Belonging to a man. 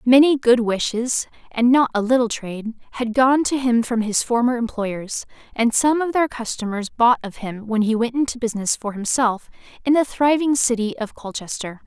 No: female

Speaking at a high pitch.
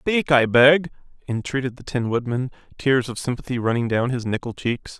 No: low, 125 Hz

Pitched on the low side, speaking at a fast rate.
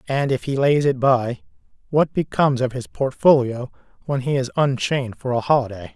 No: low, 130 Hz; average, 180 wpm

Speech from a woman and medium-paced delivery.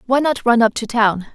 No: female; fast, 265 wpm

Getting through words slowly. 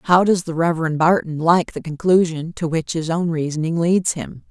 No: average, 200 wpm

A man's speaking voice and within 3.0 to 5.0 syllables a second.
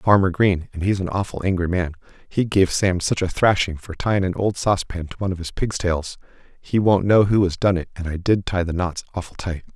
No: male; 5.8 syllables/s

